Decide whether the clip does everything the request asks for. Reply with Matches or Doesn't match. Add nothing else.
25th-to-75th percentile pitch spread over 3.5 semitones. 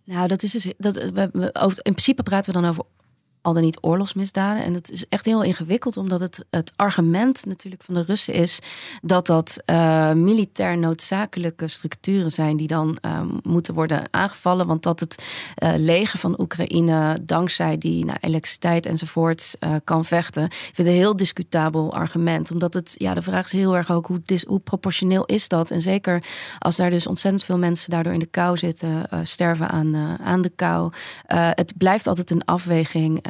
Doesn't match